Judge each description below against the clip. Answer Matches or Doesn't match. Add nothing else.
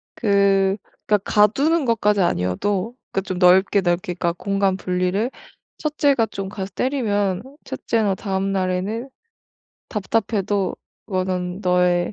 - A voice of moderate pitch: Doesn't match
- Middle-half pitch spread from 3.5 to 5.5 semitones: Doesn't match